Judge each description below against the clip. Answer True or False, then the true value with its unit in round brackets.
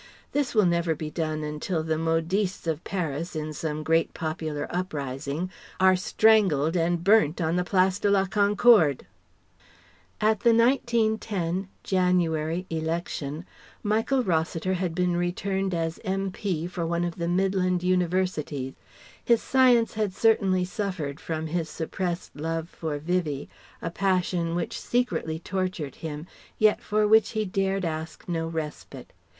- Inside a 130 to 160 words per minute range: True (140 wpm)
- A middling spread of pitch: True (3.3 semitones)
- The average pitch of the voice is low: False (175 Hz)